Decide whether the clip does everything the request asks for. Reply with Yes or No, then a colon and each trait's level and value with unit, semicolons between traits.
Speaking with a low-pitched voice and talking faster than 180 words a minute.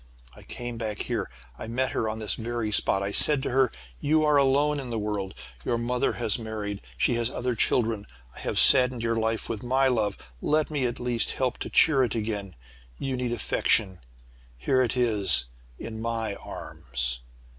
Yes: low, 115 Hz; average, 190 wpm